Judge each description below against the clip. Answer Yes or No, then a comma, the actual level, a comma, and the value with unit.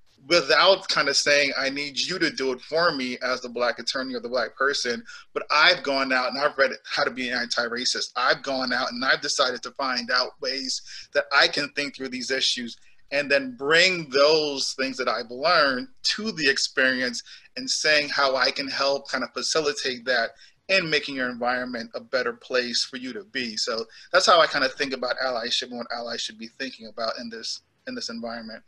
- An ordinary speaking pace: No, fast, 215 wpm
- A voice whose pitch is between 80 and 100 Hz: No, low, 130 Hz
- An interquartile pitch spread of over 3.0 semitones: No, average, 2.7 semitones